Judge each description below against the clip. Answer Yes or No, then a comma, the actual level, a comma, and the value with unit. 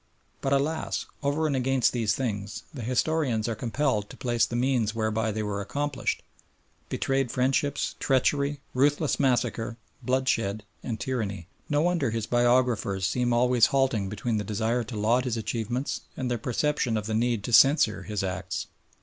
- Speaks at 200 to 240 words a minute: No, average, 160 wpm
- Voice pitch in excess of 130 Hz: No, low, 120 Hz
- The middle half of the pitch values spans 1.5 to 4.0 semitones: Yes, average, 3.5 semitones